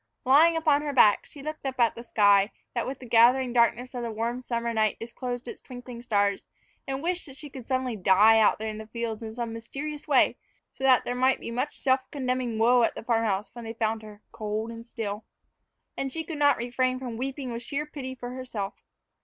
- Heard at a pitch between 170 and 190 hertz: No, high, 245 Hz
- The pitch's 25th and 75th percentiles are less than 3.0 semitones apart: Yes, narrow, 2.6 semitones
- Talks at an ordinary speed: No, fast, 225 wpm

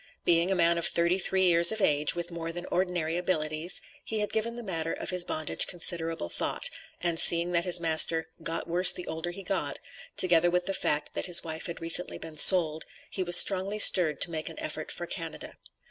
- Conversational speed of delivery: No, fast, 210 wpm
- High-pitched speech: No, medium, 170 Hz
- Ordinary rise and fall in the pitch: No, narrow, 1.9 semitones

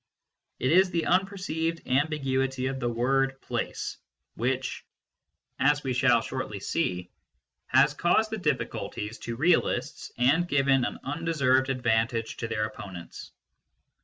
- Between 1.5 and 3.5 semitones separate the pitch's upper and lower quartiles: No, average, 4.9 semitones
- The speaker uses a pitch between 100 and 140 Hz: Yes, low, 135 Hz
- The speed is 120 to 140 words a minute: Yes, slow, 135 wpm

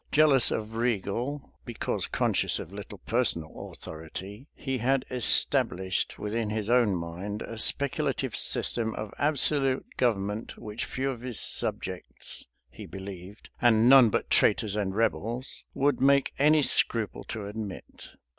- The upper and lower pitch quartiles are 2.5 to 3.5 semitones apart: No, average, 4.4 semitones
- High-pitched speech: No, low, 115 Hz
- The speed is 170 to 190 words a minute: No, slow, 135 wpm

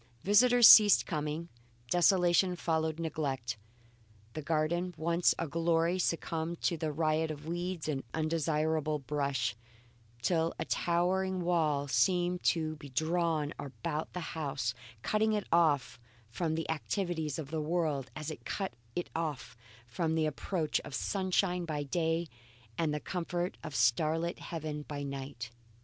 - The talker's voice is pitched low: No, medium, 160 Hz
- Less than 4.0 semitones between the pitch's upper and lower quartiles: Yes, narrow, 2.6 semitones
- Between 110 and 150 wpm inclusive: Yes, average, 145 wpm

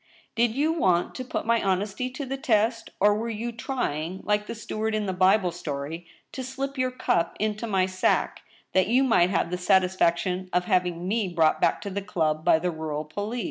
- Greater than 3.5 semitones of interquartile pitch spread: Yes, average, 4.5 semitones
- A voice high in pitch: Yes, high, 195 Hz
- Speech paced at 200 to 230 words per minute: Yes, fast, 205 wpm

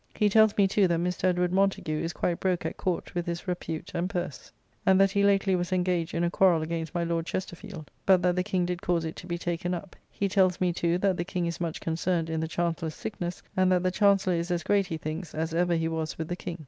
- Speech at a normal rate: No, fast, 260 wpm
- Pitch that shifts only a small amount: Yes, narrow, 1.9 semitones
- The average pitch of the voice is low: No, medium, 175 Hz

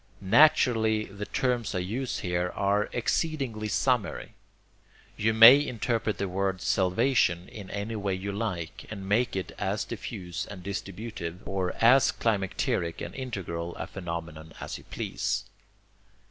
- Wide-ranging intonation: No, average, 3.9 semitones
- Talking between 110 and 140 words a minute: Yes, slow, 135 wpm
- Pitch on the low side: Yes, low, 100 Hz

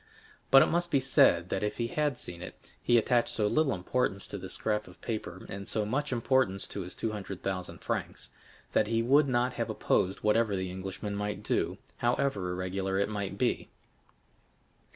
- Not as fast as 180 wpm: No, average, 190 wpm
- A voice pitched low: Yes, low, 105 Hz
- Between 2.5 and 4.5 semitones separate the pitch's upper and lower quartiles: Yes, average, 4.2 semitones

